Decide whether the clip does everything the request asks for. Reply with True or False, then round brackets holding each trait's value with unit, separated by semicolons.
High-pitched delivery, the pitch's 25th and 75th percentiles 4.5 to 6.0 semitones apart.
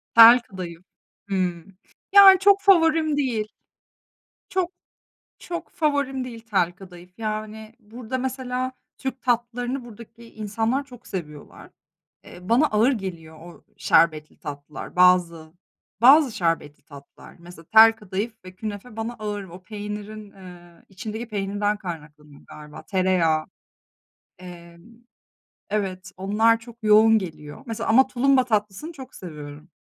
True (210 Hz; 5.4 semitones)